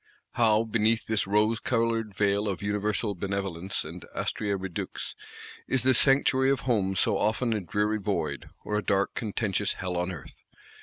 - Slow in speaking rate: No, average, 160 wpm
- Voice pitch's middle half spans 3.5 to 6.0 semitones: No, narrow, 2.6 semitones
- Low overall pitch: Yes, low, 105 Hz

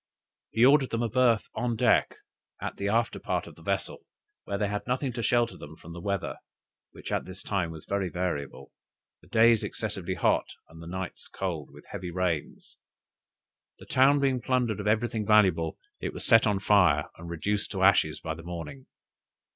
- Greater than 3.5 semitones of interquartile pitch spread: Yes, average, 5.1 semitones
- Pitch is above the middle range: No, low, 100 Hz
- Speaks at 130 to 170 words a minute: No, average, 185 wpm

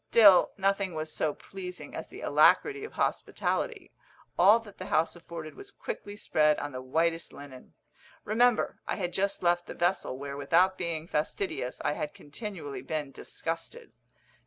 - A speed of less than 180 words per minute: Yes, average, 160 wpm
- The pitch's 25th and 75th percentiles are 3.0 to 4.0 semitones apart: No, average, 4.6 semitones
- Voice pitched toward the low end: No, medium, 175 Hz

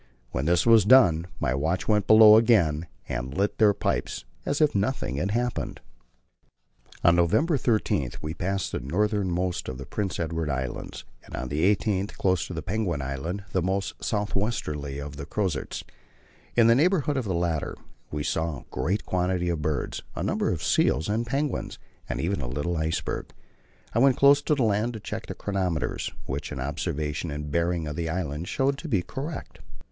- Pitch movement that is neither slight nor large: No, wide, 6.2 semitones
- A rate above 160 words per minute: Yes, average, 185 wpm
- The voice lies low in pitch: Yes, very low, 90 Hz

